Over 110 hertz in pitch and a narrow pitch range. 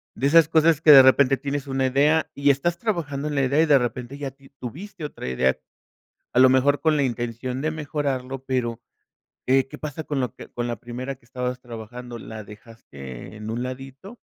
No: low, 135 Hz; average, 3.1 semitones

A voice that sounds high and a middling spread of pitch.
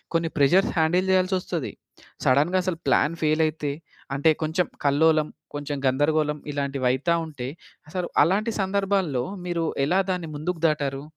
No: medium, 160 Hz; average, 3.8 semitones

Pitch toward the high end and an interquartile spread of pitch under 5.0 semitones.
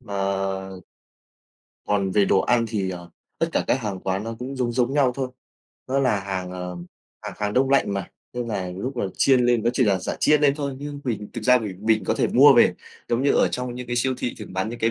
No: low, 115 Hz; average, 4.4 semitones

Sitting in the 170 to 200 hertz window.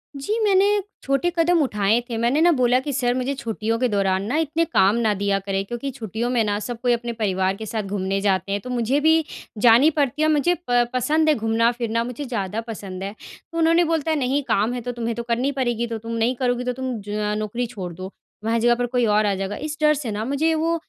No: high, 240 Hz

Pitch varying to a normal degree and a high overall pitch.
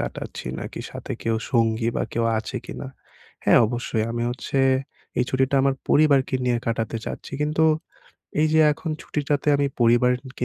No: average, 3.4 semitones; low, 125 Hz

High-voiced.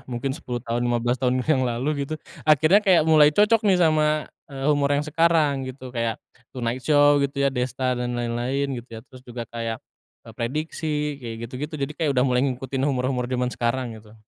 No: low, 130 Hz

